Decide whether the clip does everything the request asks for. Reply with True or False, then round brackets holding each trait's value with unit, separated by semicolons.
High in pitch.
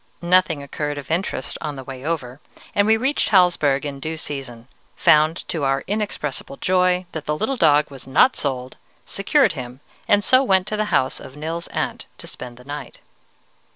False (150 Hz)